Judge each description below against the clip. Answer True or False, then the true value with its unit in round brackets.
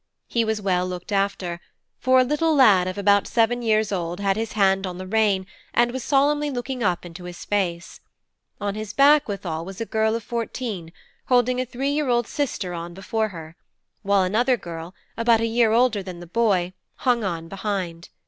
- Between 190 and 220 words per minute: True (195 wpm)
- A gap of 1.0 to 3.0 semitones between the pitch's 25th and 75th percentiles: False (4.7 semitones)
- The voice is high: True (205 Hz)